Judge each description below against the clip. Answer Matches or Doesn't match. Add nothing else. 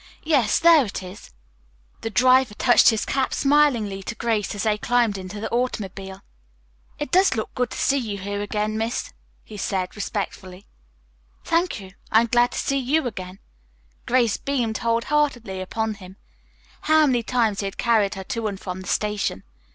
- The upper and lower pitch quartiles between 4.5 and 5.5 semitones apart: Doesn't match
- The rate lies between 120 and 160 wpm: Doesn't match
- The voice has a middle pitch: Doesn't match